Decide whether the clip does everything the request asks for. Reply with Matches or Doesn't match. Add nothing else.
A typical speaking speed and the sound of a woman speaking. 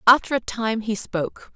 Matches